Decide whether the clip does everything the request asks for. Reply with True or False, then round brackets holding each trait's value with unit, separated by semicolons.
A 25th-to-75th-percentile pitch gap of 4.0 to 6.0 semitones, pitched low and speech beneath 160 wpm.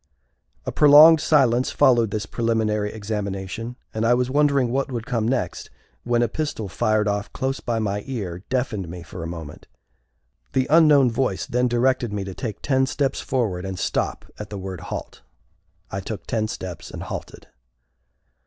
False (4.5 semitones; 115 Hz; 170 wpm)